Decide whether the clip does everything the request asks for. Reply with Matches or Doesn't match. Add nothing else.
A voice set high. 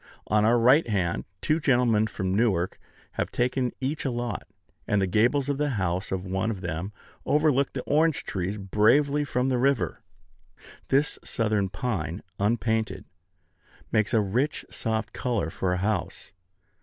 Doesn't match